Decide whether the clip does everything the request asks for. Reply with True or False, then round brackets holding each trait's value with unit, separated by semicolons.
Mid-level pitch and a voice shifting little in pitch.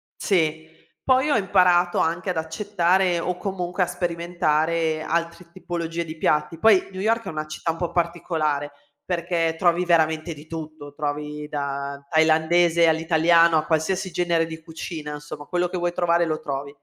True (165 Hz; 2.0 semitones)